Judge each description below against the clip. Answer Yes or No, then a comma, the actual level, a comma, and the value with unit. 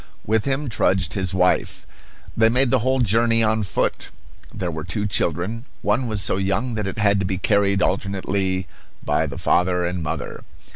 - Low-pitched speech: Yes, low, 100 Hz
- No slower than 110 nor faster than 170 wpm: No, average, 180 wpm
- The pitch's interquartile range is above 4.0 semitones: No, average, 3.3 semitones